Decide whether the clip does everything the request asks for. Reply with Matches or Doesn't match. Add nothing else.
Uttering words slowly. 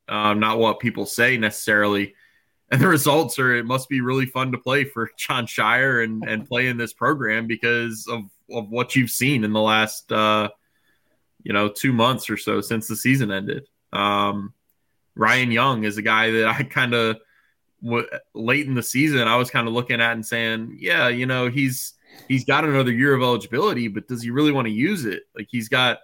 Doesn't match